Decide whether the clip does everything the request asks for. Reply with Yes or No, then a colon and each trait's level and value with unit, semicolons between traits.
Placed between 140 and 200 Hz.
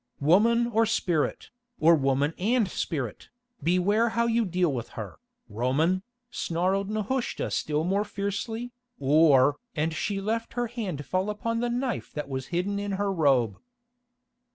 Yes: medium, 185 Hz